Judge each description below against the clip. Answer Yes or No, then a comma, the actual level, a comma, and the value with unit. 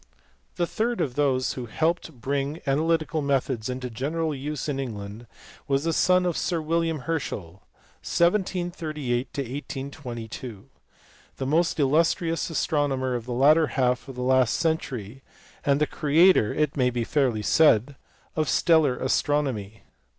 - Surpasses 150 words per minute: No, average, 145 wpm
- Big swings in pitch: No, average, 4.2 semitones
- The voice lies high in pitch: No, medium, 140 Hz